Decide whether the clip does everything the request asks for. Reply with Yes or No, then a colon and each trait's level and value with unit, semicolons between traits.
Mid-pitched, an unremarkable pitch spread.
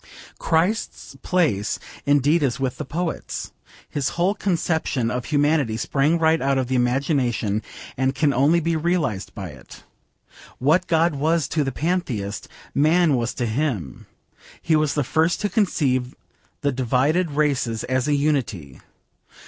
Yes: medium, 145 Hz; average, 4.5 semitones